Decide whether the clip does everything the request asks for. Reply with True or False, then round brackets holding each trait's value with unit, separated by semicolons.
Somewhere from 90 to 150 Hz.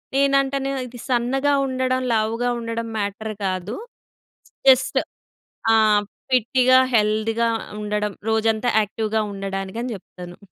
False (225 Hz)